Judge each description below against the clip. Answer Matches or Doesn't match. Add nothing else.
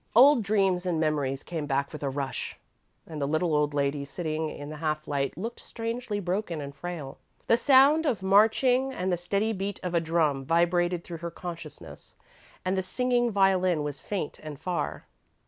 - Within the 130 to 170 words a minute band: Doesn't match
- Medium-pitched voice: Matches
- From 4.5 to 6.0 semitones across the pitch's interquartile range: Matches